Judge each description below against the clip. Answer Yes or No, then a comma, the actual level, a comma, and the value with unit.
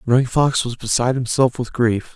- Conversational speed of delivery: Yes, average, 195 wpm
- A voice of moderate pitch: No, low, 120 Hz